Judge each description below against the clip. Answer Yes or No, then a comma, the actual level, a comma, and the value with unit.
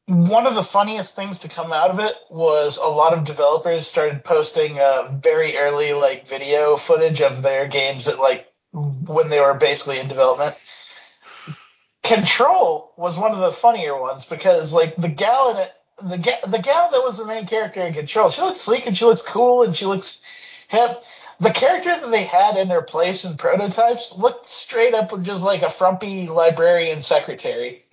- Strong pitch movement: Yes, wide, 7.2 semitones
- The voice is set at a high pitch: No, medium, 180 Hz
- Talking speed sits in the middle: Yes, average, 190 wpm